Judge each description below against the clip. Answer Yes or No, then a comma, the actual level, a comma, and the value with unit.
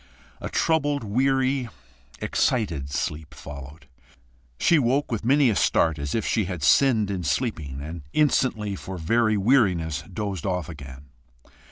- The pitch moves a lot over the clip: Yes, wide, 8.1 semitones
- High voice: No, low, 100 Hz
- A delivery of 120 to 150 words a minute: Yes, average, 140 wpm